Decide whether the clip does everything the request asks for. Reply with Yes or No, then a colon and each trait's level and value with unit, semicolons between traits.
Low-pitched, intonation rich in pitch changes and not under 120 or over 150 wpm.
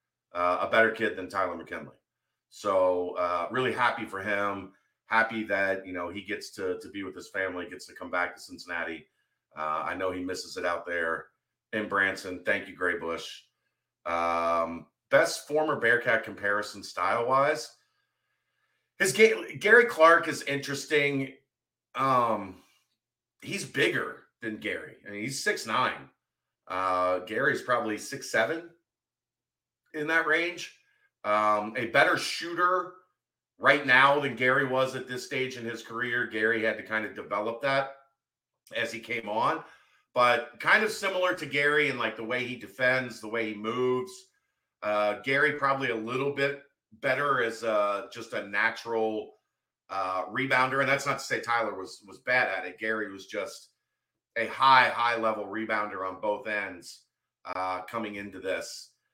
No: low, 115 Hz; wide, 6.2 semitones; average, 160 wpm